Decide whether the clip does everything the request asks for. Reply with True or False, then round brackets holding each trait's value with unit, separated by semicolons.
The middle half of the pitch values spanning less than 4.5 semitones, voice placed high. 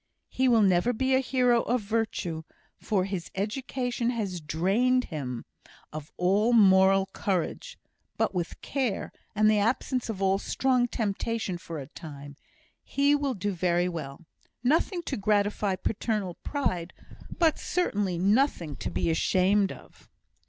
False (5.4 semitones; 205 Hz)